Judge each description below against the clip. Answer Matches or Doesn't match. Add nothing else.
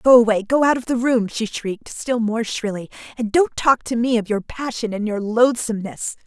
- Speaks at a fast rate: Matches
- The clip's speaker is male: Doesn't match